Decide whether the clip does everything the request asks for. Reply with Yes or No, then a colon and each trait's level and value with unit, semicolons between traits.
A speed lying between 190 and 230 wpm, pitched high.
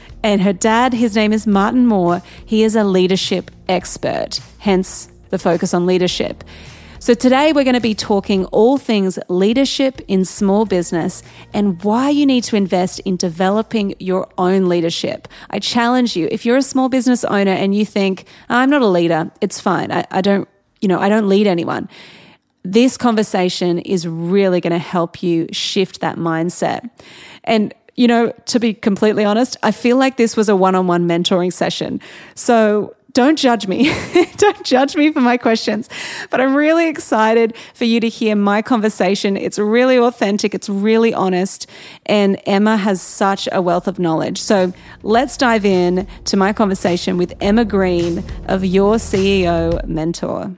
No: average, 170 wpm; high, 205 Hz